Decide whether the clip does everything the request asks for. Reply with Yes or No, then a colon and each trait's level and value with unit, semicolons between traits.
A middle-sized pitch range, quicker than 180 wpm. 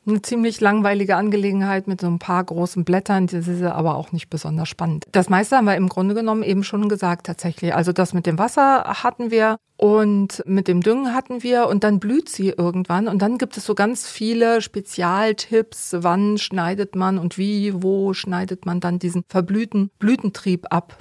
Yes: average, 3.1 semitones; fast, 190 wpm